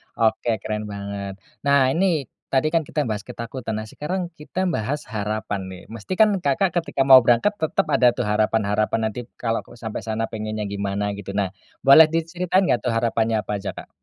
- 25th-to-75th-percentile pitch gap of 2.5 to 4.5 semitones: No, average, 5.3 semitones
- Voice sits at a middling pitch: No, low, 115 Hz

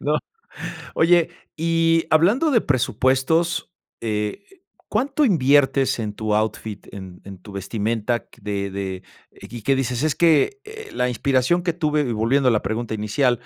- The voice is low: Yes, low, 130 Hz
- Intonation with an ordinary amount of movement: No, wide, 7.3 semitones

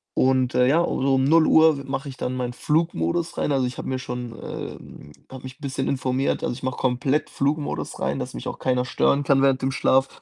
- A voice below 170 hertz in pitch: Yes, low, 135 Hz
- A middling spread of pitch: No, narrow, 1.6 semitones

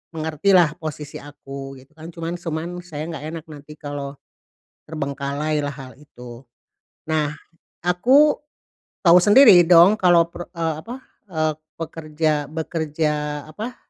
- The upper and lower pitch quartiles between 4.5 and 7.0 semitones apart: No, average, 2.9 semitones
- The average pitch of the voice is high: No, medium, 155 Hz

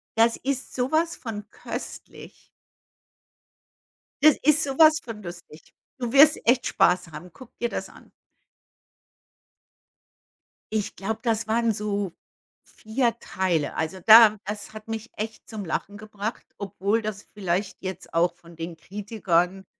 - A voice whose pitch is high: Yes, high, 215 Hz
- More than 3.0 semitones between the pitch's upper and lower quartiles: Yes, average, 3.7 semitones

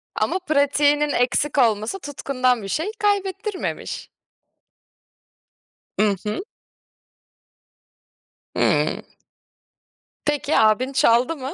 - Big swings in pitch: No, average, 4.6 semitones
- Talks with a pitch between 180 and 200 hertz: No, very high, 280 Hz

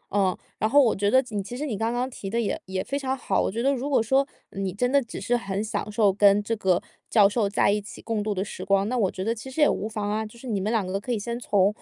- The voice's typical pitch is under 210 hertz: No, high, 215 Hz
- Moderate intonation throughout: Yes, average, 3.4 semitones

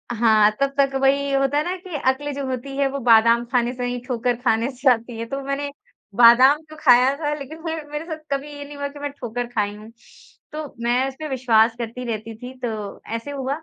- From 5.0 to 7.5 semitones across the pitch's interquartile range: No, average, 3.1 semitones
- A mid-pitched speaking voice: No, very high, 260 Hz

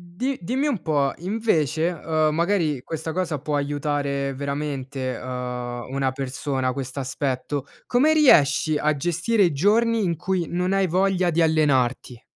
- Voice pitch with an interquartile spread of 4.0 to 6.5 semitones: Yes, average, 4.8 semitones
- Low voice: No, medium, 150 Hz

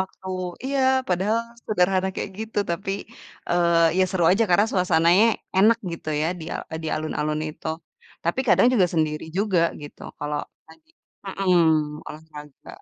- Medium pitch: Yes, medium, 175 Hz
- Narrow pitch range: No, average, 3.6 semitones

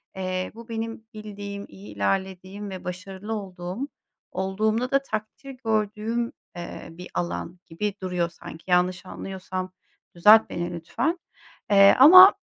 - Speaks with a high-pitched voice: Yes, high, 195 Hz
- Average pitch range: Yes, average, 3.4 semitones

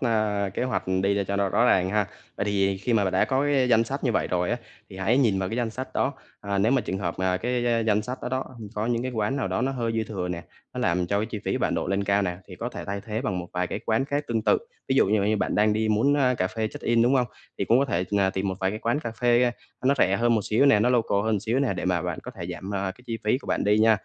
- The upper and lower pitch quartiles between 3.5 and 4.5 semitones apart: Yes, average, 3.9 semitones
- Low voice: Yes, low, 110 Hz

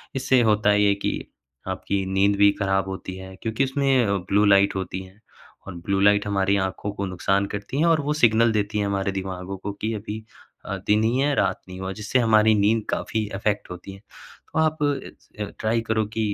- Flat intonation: Yes, narrow, 2.3 semitones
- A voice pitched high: No, low, 105 Hz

